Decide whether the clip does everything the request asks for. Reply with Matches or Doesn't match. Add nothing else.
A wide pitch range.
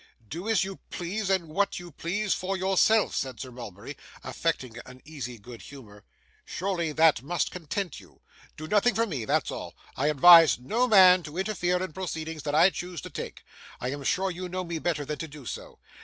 Doesn't match